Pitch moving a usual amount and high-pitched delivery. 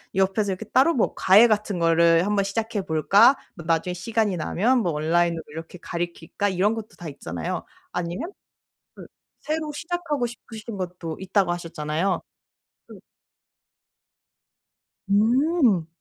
Yes: average, 5.0 semitones; high, 195 Hz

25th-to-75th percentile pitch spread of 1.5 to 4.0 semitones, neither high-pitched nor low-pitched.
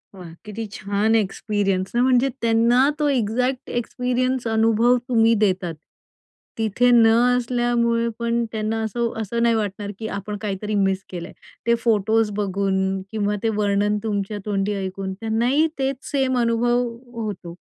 No: average, 2.9 semitones; high, 220 Hz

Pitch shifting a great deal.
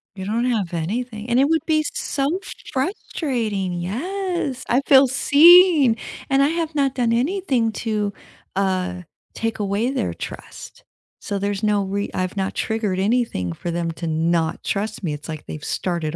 Yes: wide, 6.4 semitones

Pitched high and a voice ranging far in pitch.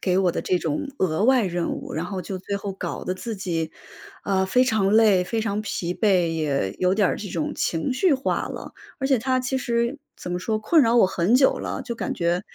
No: high, 200 Hz; average, 4.8 semitones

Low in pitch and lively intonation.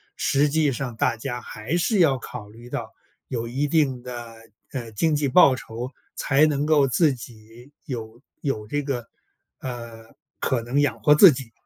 No: low, 130 Hz; average, 3.7 semitones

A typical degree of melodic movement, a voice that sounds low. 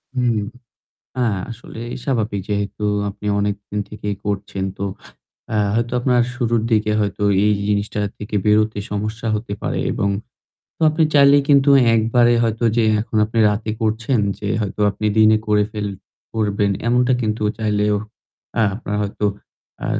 No: narrow, 2.2 semitones; low, 110 Hz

